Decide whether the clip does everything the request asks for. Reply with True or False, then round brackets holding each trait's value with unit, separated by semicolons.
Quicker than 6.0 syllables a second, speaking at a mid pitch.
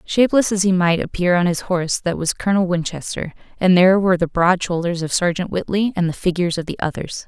True (6.3 syllables/s; 180 Hz)